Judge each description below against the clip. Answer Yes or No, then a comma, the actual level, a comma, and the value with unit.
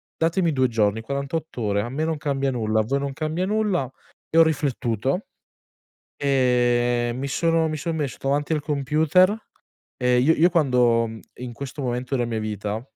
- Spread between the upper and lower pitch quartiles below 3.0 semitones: No, average, 4.6 semitones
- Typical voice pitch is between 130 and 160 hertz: Yes, low, 135 Hz